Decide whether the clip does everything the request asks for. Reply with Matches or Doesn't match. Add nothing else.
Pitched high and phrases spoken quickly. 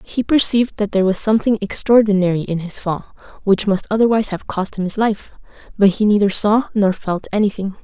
Doesn't match